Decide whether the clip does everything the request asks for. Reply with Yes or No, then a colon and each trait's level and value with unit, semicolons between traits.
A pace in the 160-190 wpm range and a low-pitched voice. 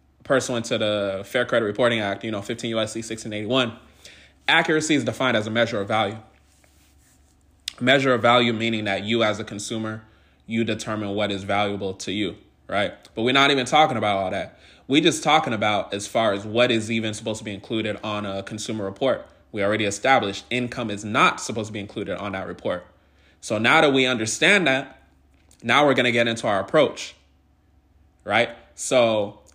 Yes: average, 185 wpm; low, 110 Hz